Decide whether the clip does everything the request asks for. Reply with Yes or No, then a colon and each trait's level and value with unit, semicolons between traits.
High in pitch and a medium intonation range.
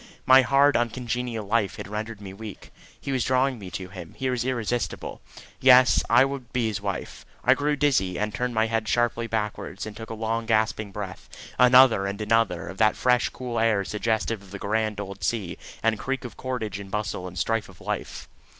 No: low, 110 Hz; average, 3.4 semitones